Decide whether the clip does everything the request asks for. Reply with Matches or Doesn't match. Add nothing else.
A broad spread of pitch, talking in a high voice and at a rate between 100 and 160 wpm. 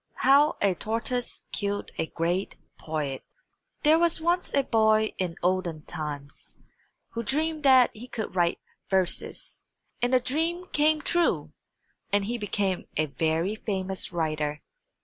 Matches